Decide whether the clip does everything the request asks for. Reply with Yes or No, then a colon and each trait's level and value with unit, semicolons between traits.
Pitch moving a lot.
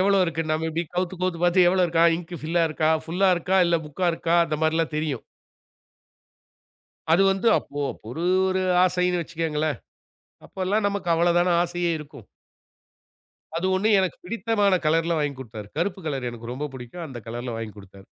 No: average, 3.5 semitones